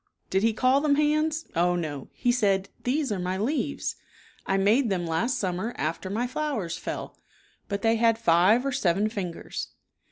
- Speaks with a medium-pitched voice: No, high, 215 Hz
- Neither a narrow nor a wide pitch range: No, wide, 5.8 semitones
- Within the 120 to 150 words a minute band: No, average, 180 wpm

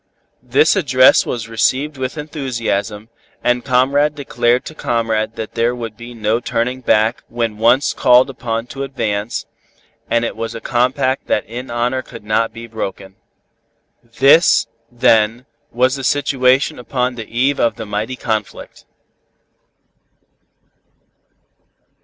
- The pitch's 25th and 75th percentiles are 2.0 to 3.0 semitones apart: Yes, narrow, 2.4 semitones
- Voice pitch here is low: Yes, low, 120 Hz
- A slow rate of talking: Yes, slow, 130 wpm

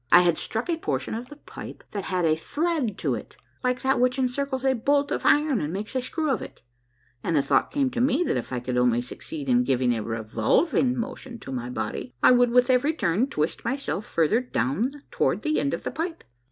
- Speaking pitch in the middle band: No, high, 245 Hz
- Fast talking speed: Yes, fast, 230 wpm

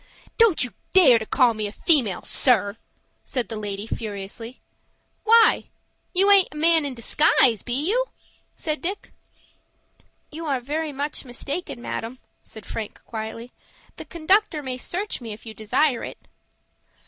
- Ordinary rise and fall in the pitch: No, wide, 6.2 semitones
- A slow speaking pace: No, average, 150 wpm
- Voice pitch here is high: Yes, very high, 260 Hz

